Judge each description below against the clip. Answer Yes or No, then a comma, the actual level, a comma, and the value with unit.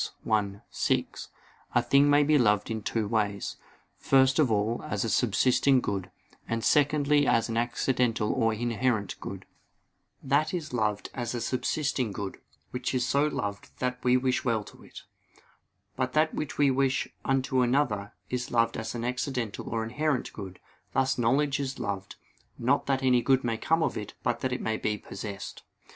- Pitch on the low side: Yes, low, 125 Hz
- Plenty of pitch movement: No, average, 3.4 semitones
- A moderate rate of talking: Yes, average, 175 wpm